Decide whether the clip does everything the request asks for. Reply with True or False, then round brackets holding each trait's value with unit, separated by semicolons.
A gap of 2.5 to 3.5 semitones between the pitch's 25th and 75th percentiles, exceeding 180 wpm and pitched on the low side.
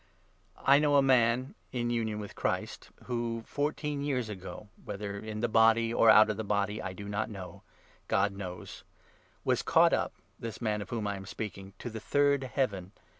True (3.1 semitones; 200 wpm; 110 Hz)